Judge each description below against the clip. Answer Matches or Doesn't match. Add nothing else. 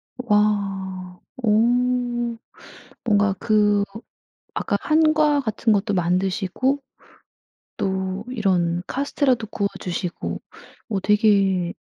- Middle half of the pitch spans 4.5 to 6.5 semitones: Doesn't match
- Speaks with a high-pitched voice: Matches